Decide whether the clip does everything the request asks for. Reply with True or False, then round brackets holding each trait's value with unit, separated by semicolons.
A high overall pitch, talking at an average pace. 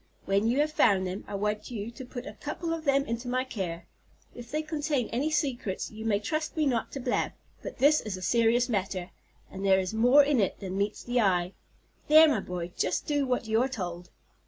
False (235 Hz; 225 wpm)